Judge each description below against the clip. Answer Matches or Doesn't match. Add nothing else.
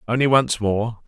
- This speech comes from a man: Matches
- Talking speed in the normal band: Matches